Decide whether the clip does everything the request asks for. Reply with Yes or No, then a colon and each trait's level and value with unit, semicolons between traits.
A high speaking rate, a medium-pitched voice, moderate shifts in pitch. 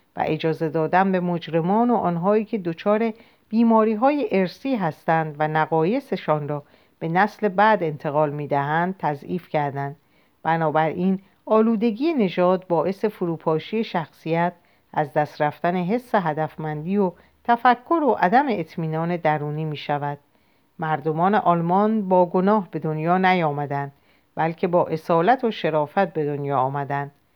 No: average, 125 wpm; medium, 170 Hz; average, 5.0 semitones